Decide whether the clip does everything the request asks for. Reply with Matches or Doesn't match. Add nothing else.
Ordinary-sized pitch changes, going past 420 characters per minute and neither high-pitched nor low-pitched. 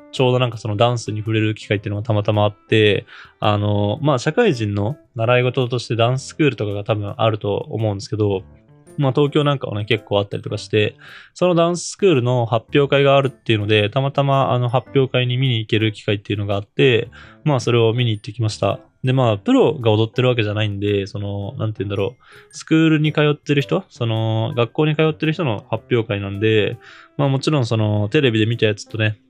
Doesn't match